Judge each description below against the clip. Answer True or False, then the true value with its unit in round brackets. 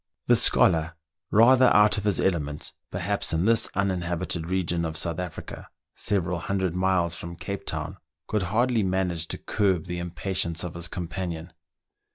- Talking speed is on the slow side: False (160 wpm)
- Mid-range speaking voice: False (90 Hz)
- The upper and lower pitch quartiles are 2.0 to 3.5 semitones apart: True (2.7 semitones)